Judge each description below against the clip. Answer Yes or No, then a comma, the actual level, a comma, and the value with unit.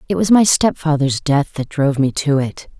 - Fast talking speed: Yes, fast, 215 wpm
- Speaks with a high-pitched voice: No, medium, 150 Hz